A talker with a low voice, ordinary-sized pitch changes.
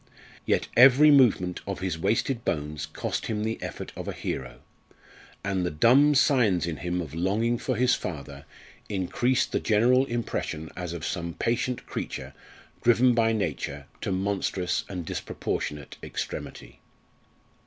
No: very low, 95 Hz; wide, 6.1 semitones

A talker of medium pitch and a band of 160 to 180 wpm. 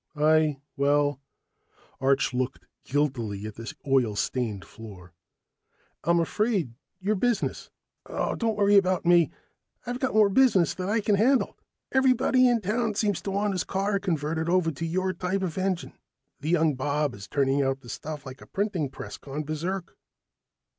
Yes: medium, 165 Hz; average, 165 wpm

